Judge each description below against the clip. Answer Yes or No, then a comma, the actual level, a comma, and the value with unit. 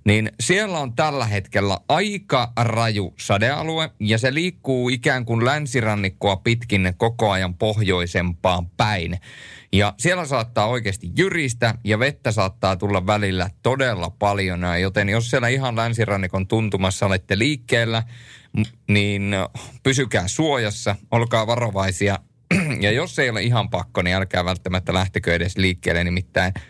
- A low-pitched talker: Yes, low, 110 Hz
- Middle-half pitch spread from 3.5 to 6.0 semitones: Yes, average, 4.3 semitones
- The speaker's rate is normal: Yes, average, 130 wpm